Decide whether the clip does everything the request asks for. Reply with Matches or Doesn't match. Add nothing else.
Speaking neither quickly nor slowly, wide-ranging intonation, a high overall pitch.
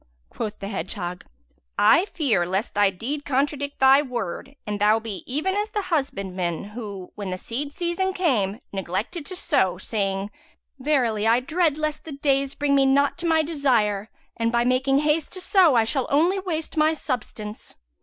Matches